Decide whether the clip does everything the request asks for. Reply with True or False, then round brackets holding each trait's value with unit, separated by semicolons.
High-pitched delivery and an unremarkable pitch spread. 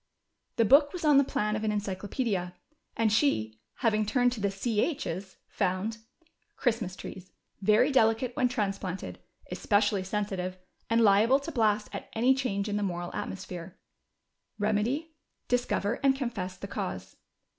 True (210 Hz; 4.2 semitones)